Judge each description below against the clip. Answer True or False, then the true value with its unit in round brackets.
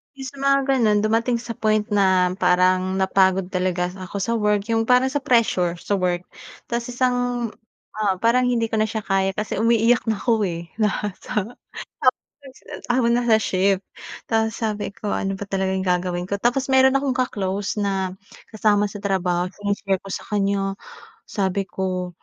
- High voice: True (205 Hz)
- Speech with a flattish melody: False (3.5 semitones)